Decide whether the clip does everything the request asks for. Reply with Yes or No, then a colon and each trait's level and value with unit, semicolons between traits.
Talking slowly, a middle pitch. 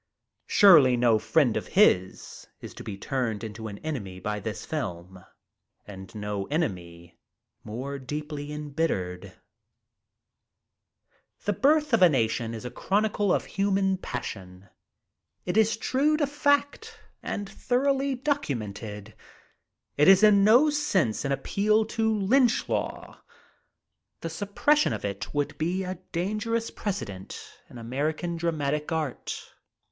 Yes: slow, 125 wpm; medium, 150 Hz